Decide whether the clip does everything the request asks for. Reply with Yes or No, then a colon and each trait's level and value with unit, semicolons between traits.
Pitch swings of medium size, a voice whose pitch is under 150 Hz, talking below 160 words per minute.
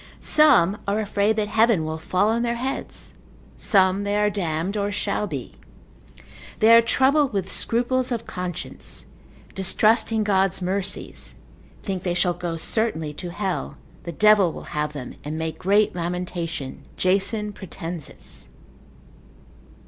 No: average, 3.8 semitones; high, 195 Hz; slow, 135 wpm